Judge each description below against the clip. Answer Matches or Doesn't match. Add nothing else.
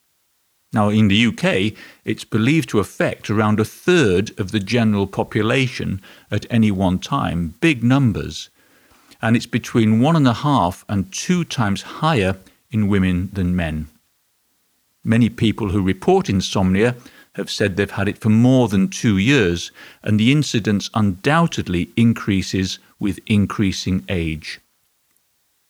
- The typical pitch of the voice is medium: Doesn't match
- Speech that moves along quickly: Doesn't match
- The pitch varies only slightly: Doesn't match